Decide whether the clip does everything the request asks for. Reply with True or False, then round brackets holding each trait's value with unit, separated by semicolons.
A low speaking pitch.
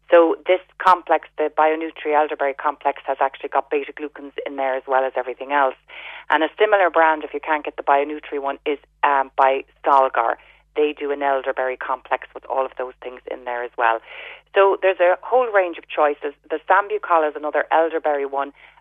False (150 Hz)